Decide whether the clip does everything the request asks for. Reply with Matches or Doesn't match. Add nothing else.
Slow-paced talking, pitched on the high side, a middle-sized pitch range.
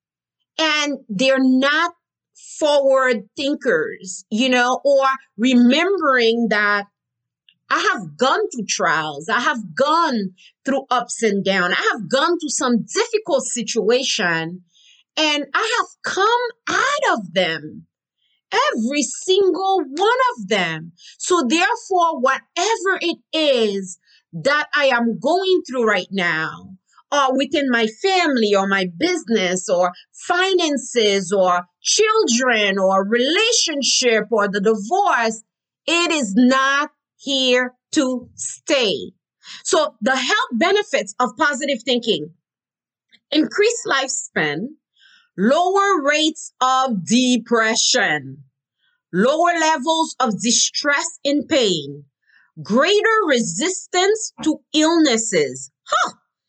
Doesn't match